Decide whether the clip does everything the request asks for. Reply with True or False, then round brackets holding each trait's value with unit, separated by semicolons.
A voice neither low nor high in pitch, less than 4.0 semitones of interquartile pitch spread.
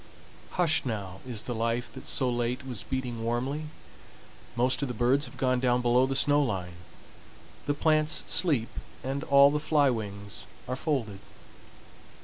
False (125 Hz; 3.3 semitones)